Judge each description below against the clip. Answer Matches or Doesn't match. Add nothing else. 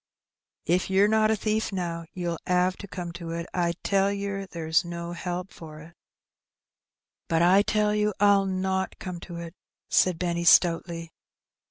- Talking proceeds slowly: Doesn't match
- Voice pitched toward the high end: Doesn't match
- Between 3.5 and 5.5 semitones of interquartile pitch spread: Doesn't match